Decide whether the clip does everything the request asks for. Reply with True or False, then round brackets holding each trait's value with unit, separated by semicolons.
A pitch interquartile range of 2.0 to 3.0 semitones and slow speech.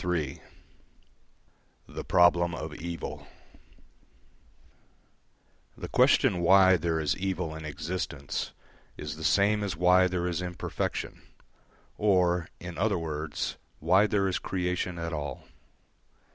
True (2.6 semitones; 115 wpm)